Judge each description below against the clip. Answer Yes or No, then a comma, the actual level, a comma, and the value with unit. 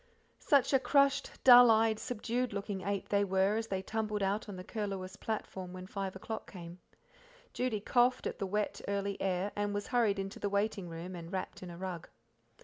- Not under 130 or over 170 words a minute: No, average, 195 wpm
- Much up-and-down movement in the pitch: No, average, 2.7 semitones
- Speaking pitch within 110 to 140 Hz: No, high, 200 Hz